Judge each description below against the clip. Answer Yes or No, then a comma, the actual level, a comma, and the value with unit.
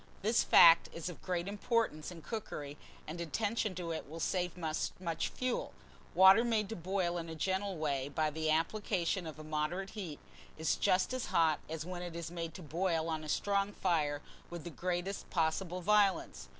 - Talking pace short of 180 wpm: No, average, 185 wpm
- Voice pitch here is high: No, medium, 175 Hz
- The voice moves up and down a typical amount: Yes, average, 3.5 semitones